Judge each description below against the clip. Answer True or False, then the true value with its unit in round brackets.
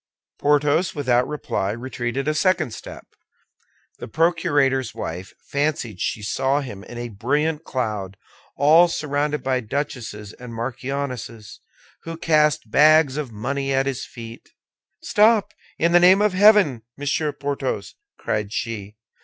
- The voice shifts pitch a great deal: False (4.7 semitones)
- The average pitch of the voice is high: False (135 Hz)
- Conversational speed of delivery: False (130 wpm)